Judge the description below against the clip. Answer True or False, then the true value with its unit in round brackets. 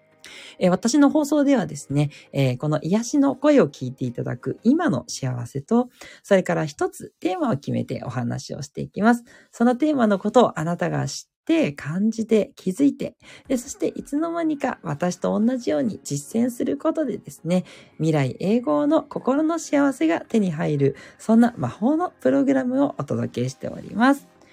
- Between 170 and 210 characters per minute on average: False (330 characters per minute)